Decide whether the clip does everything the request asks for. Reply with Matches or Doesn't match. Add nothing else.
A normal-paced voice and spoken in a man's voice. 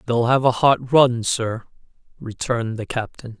Matches